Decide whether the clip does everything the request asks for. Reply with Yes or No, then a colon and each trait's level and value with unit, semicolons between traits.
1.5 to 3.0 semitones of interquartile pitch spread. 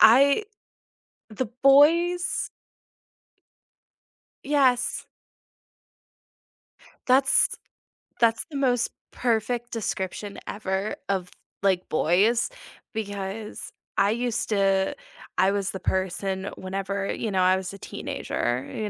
No: average, 4.3 semitones